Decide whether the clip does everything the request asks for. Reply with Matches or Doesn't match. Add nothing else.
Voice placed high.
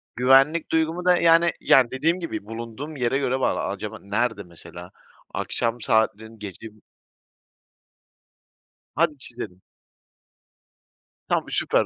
Doesn't match